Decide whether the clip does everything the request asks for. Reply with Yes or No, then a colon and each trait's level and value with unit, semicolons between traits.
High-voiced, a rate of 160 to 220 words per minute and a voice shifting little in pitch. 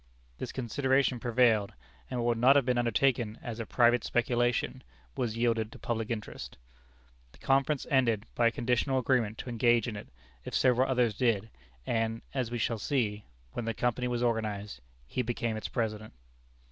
No: low, 120 Hz; average, 170 wpm; narrow, 2.0 semitones